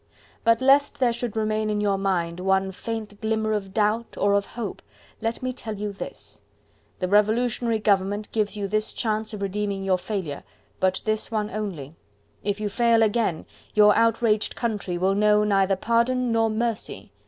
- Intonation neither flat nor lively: No, narrow, 2.2 semitones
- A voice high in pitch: Yes, high, 210 Hz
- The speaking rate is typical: Yes, average, 170 wpm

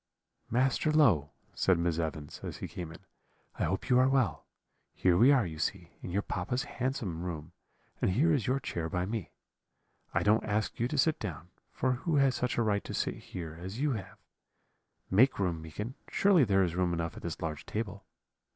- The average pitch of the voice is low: Yes, low, 100 Hz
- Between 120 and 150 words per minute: No, average, 200 wpm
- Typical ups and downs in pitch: No, wide, 6.8 semitones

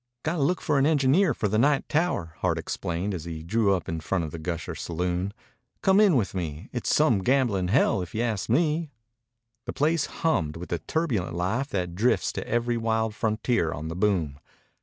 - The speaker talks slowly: No, average, 200 wpm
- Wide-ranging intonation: Yes, wide, 7.9 semitones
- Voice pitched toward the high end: No, low, 105 Hz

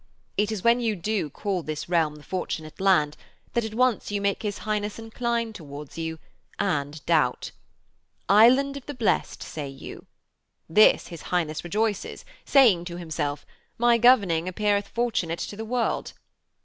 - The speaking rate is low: No, average, 155 wpm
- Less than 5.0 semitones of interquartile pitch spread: No, wide, 5.6 semitones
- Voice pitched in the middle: No, high, 200 Hz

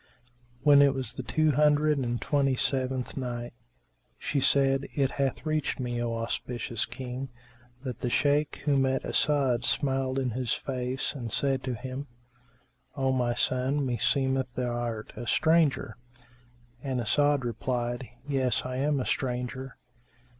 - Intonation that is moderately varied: No, narrow, 2.1 semitones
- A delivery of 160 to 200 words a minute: No, average, 145 wpm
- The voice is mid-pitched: No, low, 130 Hz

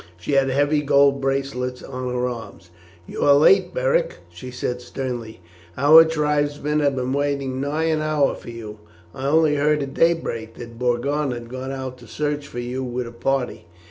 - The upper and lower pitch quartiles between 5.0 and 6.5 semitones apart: No, average, 3.0 semitones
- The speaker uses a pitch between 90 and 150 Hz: Yes, low, 135 Hz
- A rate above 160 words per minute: Yes, average, 180 wpm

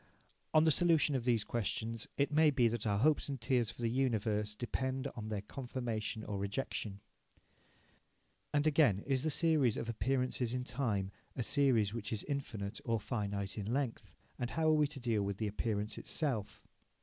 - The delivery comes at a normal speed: Yes, average, 180 wpm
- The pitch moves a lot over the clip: No, average, 4.3 semitones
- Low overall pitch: Yes, low, 120 Hz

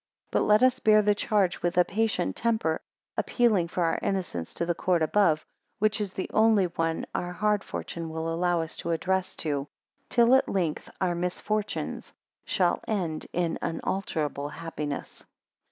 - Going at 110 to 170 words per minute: Yes, average, 165 wpm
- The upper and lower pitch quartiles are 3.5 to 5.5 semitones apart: Yes, average, 4.2 semitones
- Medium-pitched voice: Yes, medium, 180 Hz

